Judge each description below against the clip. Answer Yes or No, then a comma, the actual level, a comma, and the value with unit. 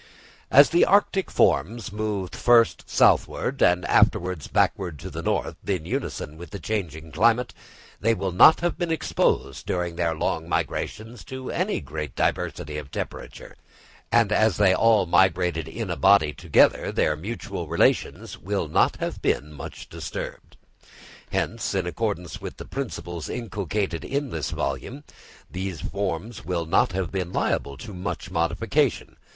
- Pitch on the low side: Yes, very low, 95 Hz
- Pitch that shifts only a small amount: No, average, 5.2 semitones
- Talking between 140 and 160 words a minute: Yes, average, 150 wpm